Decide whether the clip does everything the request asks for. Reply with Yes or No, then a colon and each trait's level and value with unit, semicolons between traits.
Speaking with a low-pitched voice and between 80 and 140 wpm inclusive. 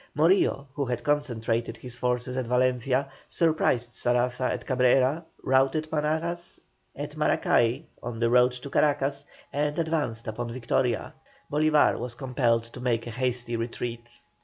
Yes: low, 125 Hz; slow, 135 wpm